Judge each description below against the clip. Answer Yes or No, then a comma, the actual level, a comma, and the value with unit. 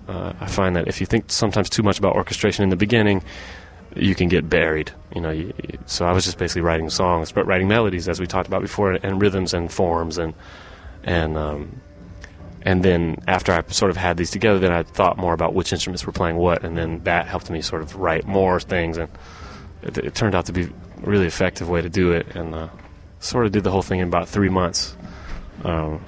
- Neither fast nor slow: No, fast, 235 wpm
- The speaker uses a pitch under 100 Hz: Yes, very low, 90 Hz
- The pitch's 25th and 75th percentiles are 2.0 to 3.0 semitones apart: Yes, narrow, 2.4 semitones